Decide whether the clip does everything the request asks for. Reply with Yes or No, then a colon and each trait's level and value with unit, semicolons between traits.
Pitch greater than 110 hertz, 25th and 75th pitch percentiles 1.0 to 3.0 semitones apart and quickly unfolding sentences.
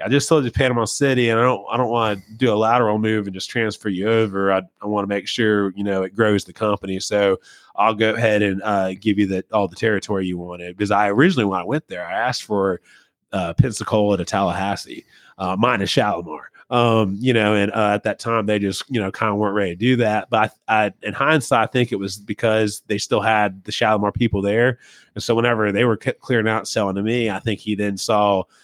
No: low, 105 Hz; narrow, 2.4 semitones; fast, 245 wpm